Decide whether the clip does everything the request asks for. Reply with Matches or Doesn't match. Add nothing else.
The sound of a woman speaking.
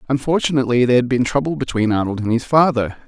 Doesn't match